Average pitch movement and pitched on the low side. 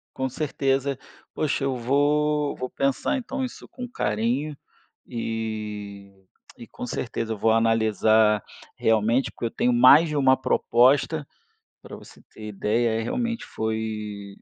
Yes: average, 4.4 semitones; low, 120 Hz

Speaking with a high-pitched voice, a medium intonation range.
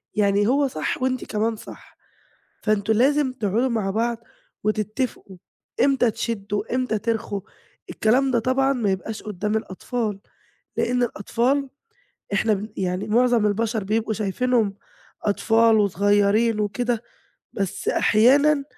Yes: high, 220 Hz; average, 3.2 semitones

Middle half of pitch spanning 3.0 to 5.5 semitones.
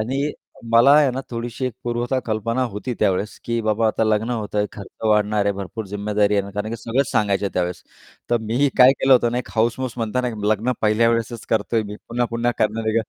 No: narrow, 2.5 semitones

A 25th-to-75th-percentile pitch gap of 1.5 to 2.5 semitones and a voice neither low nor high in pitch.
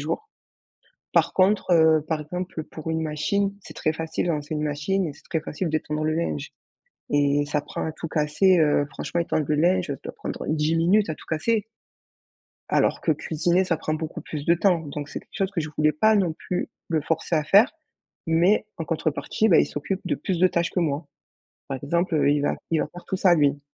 No: average, 2.9 semitones; medium, 160 Hz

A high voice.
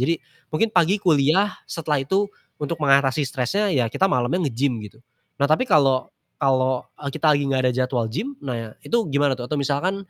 No: medium, 140 Hz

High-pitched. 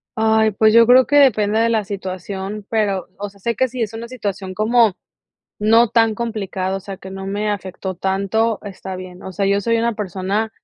Yes: high, 210 Hz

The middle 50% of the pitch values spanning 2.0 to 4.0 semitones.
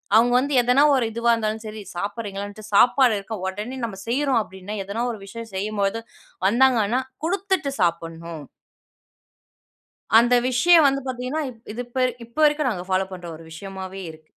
No: average, 4.4 semitones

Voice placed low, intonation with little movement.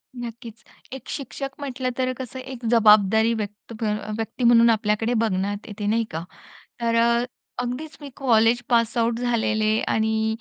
No: high, 230 Hz; narrow, 1.9 semitones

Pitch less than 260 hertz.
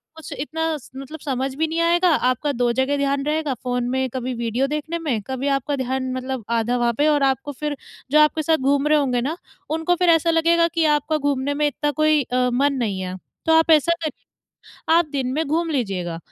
No: very high, 280 Hz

